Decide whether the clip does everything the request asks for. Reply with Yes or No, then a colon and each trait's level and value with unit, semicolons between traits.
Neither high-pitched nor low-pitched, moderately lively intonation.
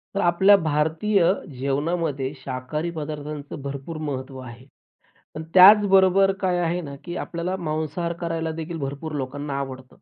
Yes: medium, 155 Hz; average, 3.8 semitones